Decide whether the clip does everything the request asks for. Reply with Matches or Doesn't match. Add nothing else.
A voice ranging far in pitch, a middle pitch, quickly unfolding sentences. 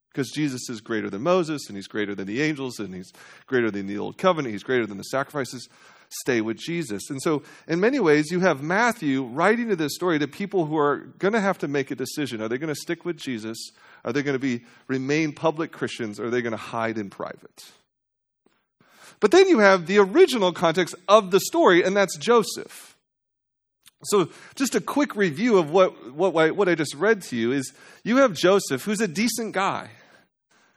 Matches